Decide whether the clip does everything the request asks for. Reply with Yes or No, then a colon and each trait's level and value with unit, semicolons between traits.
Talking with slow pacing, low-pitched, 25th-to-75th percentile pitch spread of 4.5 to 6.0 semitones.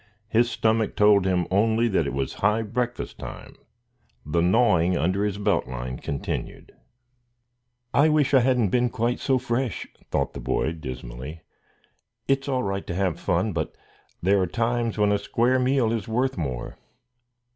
No: average, 160 wpm; low, 105 Hz; wide, 5.6 semitones